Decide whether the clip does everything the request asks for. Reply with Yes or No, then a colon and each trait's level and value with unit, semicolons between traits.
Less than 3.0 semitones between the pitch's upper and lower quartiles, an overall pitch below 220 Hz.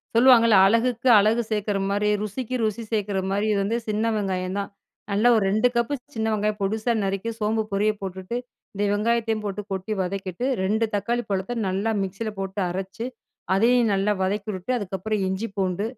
Yes: narrow, 2.6 semitones; high, 210 Hz